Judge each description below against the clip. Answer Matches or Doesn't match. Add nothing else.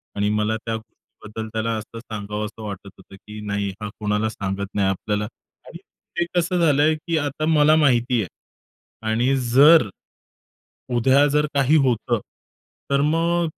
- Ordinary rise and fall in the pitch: Doesn't match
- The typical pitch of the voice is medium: Doesn't match